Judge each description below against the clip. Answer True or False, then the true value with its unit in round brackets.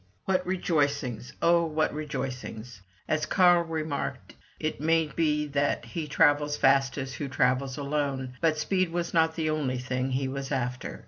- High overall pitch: False (145 Hz)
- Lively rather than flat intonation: False (3.3 semitones)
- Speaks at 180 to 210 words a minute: False (150 wpm)